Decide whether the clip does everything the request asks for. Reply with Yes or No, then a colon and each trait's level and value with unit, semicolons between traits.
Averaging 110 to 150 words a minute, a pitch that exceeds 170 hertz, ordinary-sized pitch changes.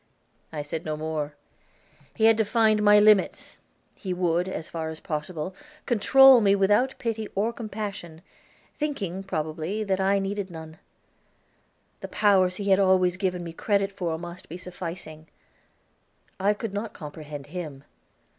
Yes: average, 145 wpm; medium, 185 Hz; average, 4.2 semitones